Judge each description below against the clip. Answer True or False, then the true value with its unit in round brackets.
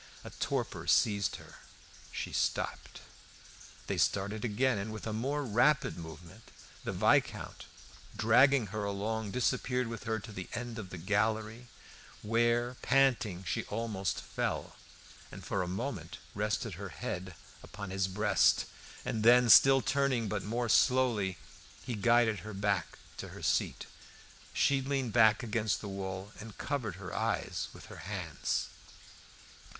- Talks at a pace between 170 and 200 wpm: False (145 wpm)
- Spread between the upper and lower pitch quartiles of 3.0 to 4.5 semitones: True (3.4 semitones)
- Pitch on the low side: True (110 Hz)